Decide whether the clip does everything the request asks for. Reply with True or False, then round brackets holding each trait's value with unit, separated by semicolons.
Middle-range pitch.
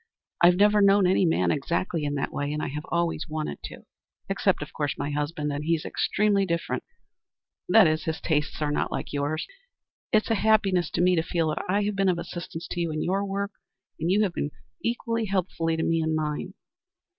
True (170 Hz)